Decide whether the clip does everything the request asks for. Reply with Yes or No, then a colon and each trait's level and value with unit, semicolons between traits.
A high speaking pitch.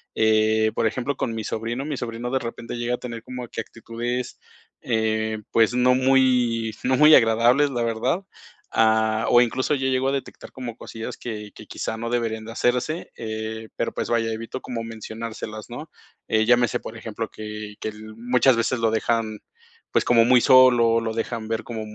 No: low, 115 Hz